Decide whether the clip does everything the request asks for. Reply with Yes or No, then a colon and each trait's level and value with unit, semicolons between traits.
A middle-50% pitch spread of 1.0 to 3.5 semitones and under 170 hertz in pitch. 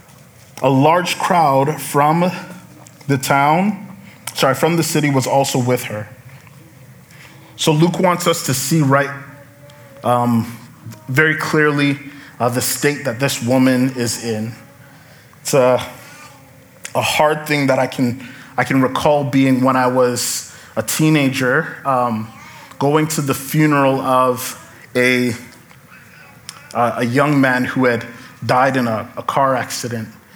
Yes: average, 2.7 semitones; low, 135 Hz